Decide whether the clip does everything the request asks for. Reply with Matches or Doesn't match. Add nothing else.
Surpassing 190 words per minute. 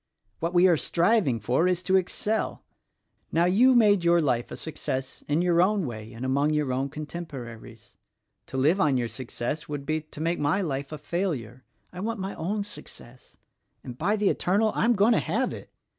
Matches